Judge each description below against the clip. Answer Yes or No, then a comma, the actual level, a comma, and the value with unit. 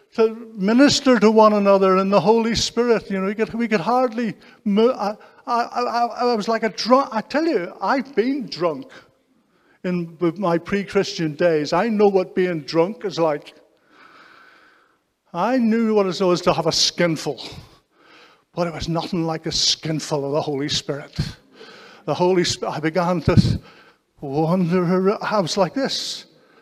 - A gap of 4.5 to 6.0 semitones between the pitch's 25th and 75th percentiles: Yes, average, 5.3 semitones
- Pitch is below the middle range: No, high, 195 Hz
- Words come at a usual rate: Yes, average, 165 wpm